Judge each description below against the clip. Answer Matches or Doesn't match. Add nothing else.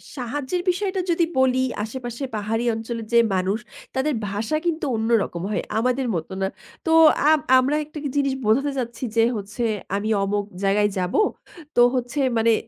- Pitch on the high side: Matches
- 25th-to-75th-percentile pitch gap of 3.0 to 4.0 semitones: Doesn't match